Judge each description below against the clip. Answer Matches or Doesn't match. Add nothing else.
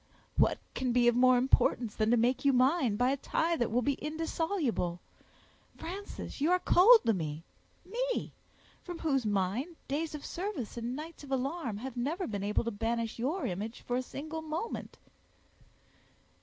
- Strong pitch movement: Matches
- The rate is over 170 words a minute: Doesn't match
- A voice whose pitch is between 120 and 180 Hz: Doesn't match